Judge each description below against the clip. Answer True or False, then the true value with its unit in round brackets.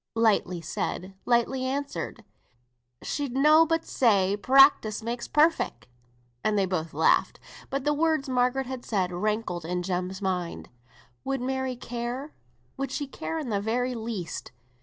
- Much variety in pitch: True (5.9 semitones)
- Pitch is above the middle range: True (240 Hz)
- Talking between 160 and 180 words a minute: False (140 wpm)